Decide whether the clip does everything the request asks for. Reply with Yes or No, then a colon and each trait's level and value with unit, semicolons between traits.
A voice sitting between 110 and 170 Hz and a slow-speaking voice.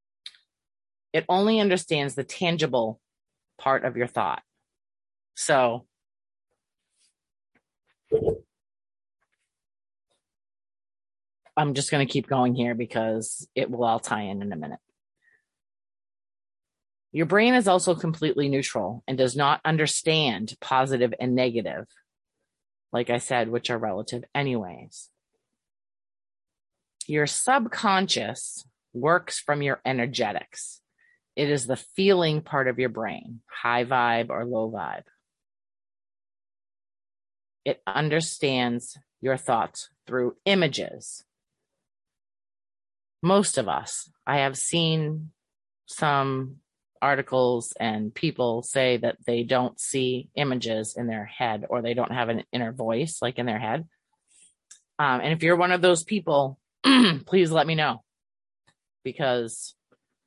Yes: low, 135 Hz; slow, 115 wpm